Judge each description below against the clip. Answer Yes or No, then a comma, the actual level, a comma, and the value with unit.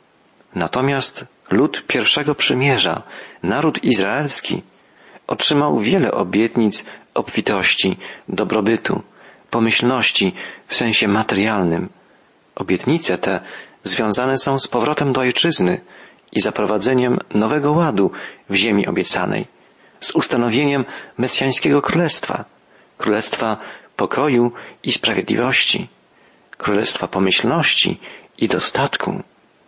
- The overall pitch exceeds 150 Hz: No, low, 125 Hz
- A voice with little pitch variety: No, average, 4.4 semitones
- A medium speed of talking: No, slow, 85 wpm